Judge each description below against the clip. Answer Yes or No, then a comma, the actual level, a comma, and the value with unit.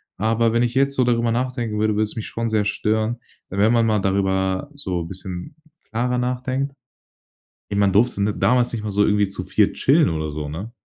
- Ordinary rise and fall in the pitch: Yes, average, 3.5 semitones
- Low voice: Yes, low, 110 Hz